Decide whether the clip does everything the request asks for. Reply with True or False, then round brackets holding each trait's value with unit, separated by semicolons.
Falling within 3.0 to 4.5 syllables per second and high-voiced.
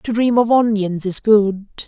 True (4.2 syllables/s; 215 Hz)